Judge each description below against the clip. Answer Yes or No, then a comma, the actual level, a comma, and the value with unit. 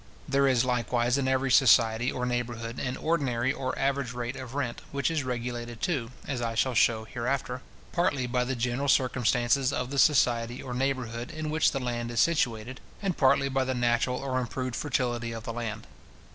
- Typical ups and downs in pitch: No, narrow, 2.2 semitones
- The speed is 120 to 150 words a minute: No, average, 185 wpm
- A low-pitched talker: Yes, low, 125 Hz